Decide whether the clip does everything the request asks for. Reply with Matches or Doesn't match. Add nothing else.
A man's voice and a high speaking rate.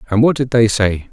Matches